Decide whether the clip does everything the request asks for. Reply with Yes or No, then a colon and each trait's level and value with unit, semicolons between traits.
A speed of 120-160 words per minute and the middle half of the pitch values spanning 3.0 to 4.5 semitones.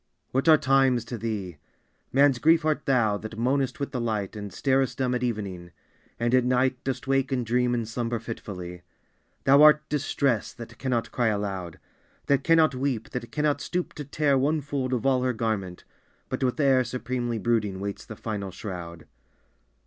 No: average, 185 wpm; average, 3.8 semitones